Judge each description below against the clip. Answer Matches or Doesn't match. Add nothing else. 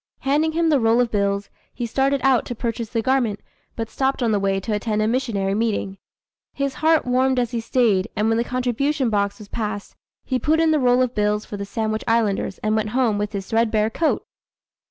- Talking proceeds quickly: Matches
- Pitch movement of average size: Matches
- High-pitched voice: Matches